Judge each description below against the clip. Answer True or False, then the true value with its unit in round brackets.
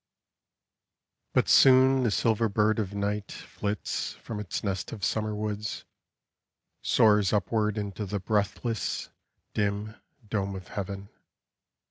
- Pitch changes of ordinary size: False (1.4 semitones)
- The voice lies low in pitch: True (105 Hz)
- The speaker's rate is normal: False (115 wpm)